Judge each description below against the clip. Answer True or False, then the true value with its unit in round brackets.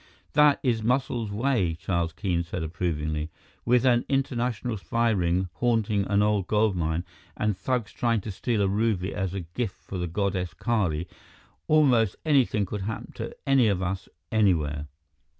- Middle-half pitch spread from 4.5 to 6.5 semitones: True (4.8 semitones)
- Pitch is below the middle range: True (105 Hz)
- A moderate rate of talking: True (160 wpm)